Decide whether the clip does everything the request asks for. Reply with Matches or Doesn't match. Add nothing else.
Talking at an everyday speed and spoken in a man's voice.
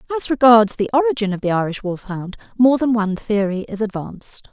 Doesn't match